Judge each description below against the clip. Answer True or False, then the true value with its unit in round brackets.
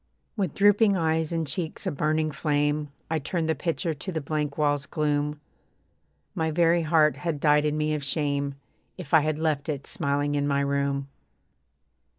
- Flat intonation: True (2.0 semitones)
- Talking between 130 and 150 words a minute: False (170 wpm)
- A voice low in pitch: False (150 Hz)